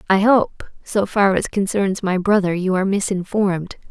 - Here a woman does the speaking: Yes, female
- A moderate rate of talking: Yes, average, 170 wpm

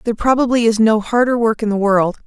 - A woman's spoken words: Yes, female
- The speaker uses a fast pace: Yes, fast, 240 wpm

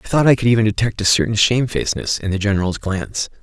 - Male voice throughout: Yes, male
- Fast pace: Yes, fast, 230 wpm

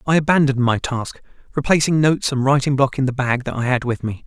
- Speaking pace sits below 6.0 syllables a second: No, 6.3 syllables/s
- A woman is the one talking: No, male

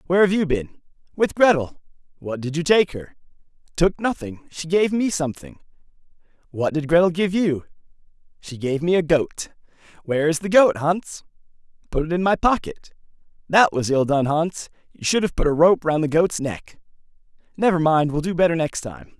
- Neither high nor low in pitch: Yes, medium, 165 Hz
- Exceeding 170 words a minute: Yes, average, 185 wpm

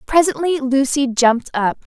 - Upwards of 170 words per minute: No, slow, 125 wpm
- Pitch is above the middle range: Yes, very high, 270 Hz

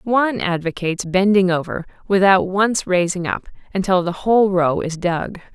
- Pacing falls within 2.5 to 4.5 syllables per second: No, 5.0 syllables/s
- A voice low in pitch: No, medium, 185 Hz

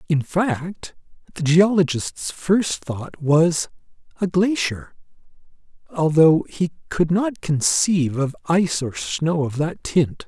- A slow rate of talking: Yes, slow, 125 wpm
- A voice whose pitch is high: No, medium, 165 Hz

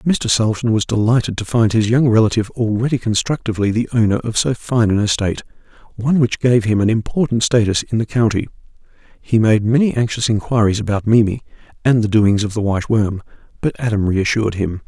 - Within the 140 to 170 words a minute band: No, average, 180 wpm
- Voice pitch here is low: Yes, low, 110 Hz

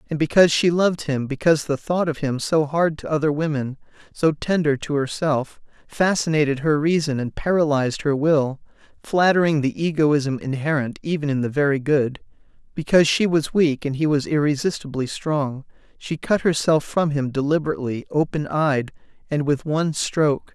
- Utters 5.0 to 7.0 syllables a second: Yes, 5.2 syllables/s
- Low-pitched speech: No, medium, 150 Hz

